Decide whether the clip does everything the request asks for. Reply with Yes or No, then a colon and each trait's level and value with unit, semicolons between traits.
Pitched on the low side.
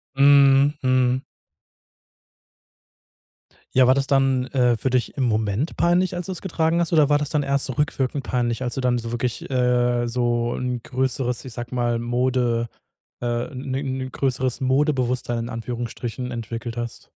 Yes: low, 125 Hz